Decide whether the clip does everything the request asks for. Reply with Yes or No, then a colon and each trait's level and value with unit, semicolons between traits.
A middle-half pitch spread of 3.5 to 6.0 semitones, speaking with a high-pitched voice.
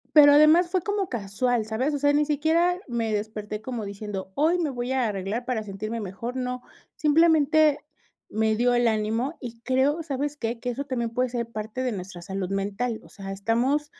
Yes: average, 5.1 semitones; high, 245 Hz